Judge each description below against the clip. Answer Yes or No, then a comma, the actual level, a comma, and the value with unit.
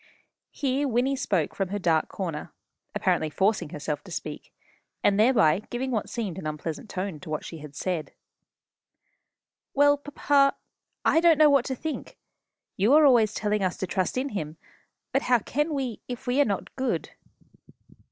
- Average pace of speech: Yes, average, 165 wpm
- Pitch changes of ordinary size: No, wide, 7.4 semitones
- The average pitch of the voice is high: Yes, high, 220 Hz